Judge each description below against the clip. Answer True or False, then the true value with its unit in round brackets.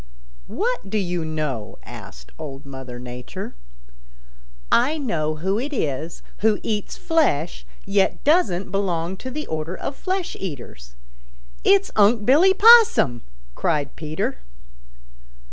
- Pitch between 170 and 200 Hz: True (190 Hz)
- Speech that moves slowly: True (120 wpm)